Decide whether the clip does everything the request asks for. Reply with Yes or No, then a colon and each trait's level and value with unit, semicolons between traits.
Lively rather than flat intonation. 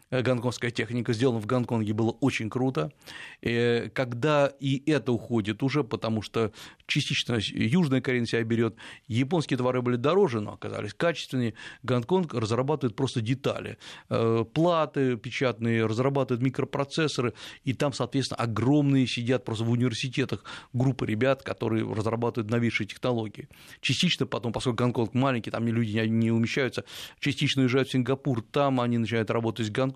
No: average, 2.8 semitones